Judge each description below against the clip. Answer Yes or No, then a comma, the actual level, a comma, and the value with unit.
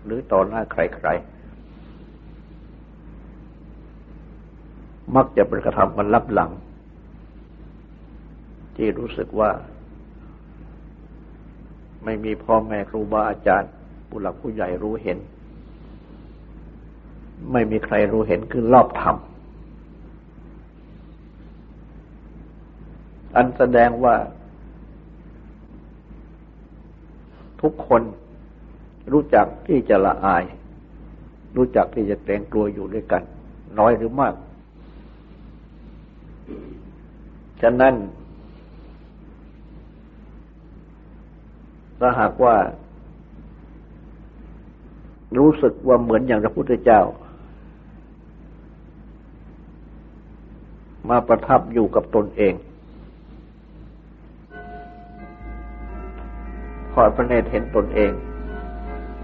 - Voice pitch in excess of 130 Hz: No, low, 105 Hz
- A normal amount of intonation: No, wide, 7.0 semitones